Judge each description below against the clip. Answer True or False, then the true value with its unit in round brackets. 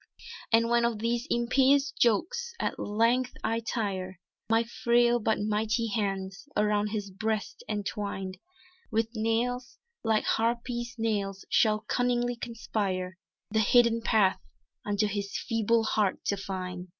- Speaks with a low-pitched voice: False (225 Hz)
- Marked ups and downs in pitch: False (2.6 semitones)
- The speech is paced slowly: True (125 wpm)